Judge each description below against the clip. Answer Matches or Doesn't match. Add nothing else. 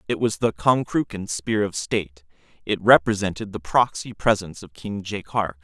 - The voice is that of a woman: Doesn't match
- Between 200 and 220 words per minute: Doesn't match